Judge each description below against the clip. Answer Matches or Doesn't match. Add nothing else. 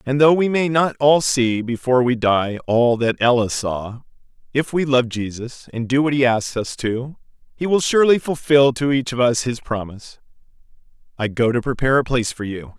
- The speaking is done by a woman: Doesn't match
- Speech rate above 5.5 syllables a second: Doesn't match